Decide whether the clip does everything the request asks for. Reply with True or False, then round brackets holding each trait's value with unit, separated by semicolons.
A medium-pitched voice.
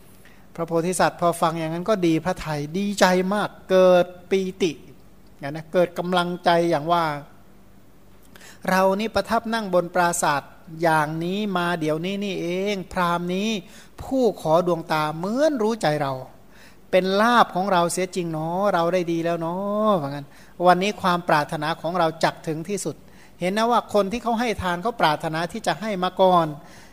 True (180 Hz)